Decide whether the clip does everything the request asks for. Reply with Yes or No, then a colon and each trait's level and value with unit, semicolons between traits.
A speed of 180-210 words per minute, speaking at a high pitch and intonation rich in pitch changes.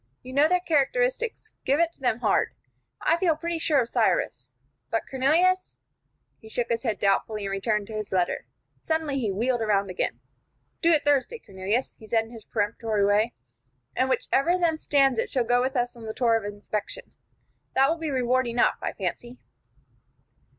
Yes: average, 190 wpm; high, 245 Hz; wide, 6.0 semitones